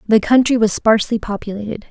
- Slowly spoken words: No, average, 155 wpm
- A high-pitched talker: Yes, high, 220 Hz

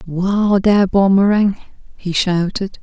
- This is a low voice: No, high, 190 Hz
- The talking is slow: Yes, slow, 105 wpm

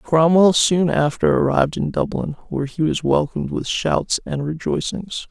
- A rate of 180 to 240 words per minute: No, average, 160 wpm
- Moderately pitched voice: Yes, medium, 160 Hz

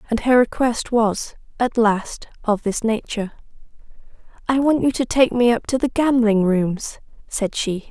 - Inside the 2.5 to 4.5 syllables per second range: Yes, 4.4 syllables/s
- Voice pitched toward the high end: Yes, high, 230 Hz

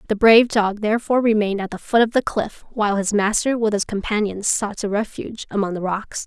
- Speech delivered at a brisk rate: Yes, fast, 220 wpm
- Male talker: No, female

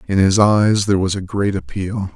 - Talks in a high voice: No, low, 100 Hz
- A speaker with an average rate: No, fast, 225 wpm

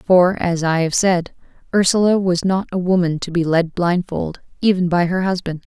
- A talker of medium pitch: Yes, medium, 180 Hz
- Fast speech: No, average, 190 wpm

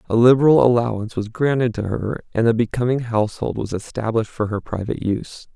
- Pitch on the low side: Yes, low, 115 Hz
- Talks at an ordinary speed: Yes, average, 185 wpm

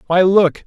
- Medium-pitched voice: Yes, medium, 180 Hz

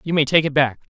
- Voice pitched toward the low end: No, medium, 145 Hz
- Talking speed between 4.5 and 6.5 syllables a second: No, 6.9 syllables/s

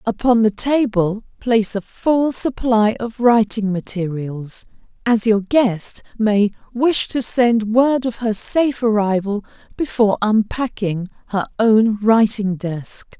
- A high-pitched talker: Yes, high, 220 Hz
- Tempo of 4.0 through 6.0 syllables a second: No, 3.8 syllables/s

